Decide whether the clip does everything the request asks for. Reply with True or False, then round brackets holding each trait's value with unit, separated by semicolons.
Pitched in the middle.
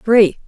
False (215 Hz)